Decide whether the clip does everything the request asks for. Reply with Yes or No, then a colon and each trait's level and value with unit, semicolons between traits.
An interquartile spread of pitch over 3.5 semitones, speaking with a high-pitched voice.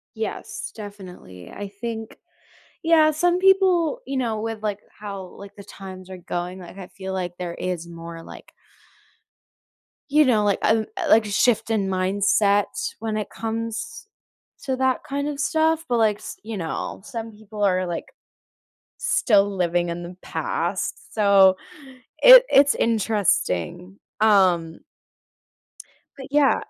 Yes: average, 4.9 semitones; high, 210 Hz